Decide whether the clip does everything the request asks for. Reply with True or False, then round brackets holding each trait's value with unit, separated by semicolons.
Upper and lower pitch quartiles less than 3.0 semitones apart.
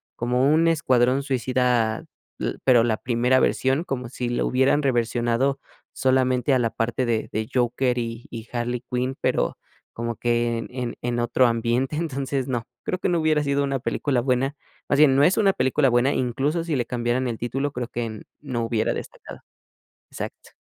True (2.4 semitones)